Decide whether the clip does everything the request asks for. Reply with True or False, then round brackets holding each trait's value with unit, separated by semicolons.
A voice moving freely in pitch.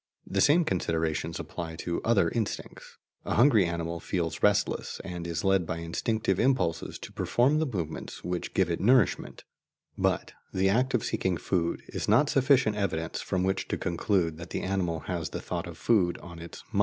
False (4.8 semitones)